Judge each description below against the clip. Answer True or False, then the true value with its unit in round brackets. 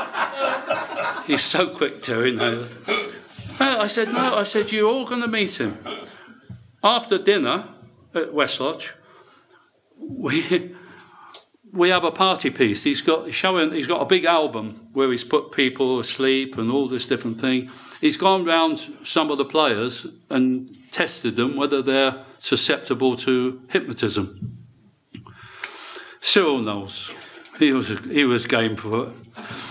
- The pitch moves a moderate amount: False (6.9 semitones)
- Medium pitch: True (145 Hz)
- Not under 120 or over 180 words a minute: True (140 wpm)